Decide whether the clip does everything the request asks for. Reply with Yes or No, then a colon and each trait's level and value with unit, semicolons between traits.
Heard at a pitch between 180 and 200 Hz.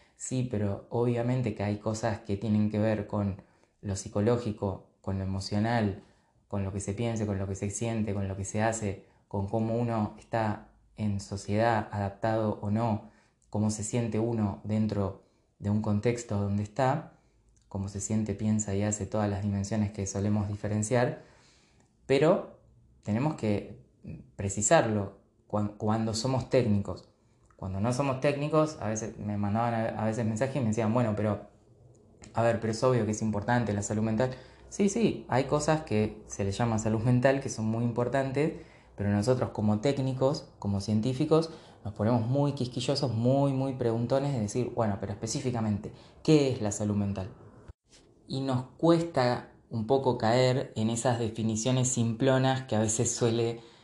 No: low, 110 Hz